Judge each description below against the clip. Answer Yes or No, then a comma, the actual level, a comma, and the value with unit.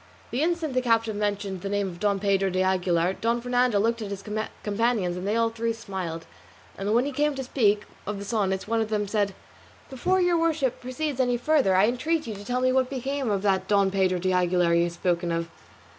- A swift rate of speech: Yes, fast, 225 wpm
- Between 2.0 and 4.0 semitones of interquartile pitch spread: No, average, 4.7 semitones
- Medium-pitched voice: No, high, 210 Hz